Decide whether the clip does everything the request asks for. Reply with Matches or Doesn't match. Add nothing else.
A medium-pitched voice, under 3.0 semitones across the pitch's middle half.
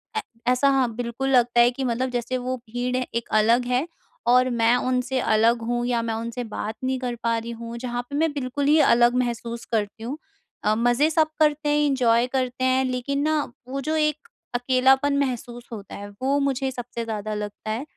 Doesn't match